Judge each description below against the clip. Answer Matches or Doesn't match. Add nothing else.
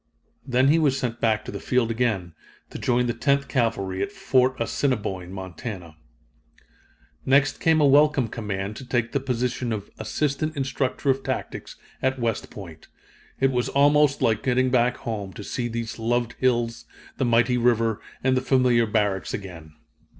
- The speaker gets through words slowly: Doesn't match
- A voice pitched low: Matches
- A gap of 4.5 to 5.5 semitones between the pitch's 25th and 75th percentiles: Doesn't match